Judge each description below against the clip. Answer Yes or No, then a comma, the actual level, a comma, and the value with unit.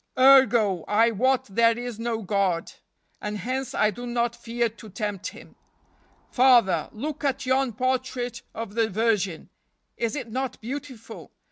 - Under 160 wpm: Yes, average, 145 wpm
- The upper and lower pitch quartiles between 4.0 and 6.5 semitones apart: No, average, 3.2 semitones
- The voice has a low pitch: No, high, 235 Hz